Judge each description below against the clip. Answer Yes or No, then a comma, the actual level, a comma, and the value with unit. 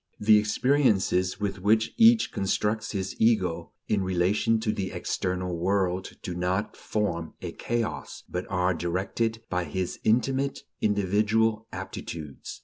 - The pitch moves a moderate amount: Yes, average, 3.4 semitones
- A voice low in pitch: Yes, low, 100 Hz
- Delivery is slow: Yes, slow, 130 wpm